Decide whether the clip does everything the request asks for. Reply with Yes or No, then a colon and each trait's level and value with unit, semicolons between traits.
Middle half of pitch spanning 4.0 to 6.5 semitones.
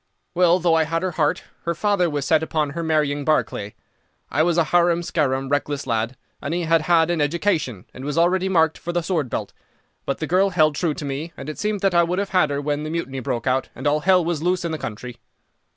No: average, 3.2 semitones